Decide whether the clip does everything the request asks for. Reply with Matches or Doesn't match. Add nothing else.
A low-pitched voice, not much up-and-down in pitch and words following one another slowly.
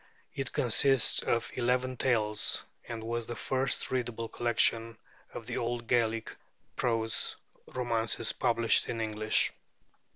Matches